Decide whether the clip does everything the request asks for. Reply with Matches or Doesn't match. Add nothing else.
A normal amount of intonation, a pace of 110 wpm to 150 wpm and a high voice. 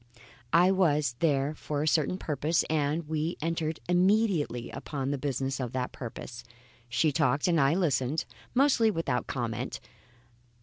Doesn't match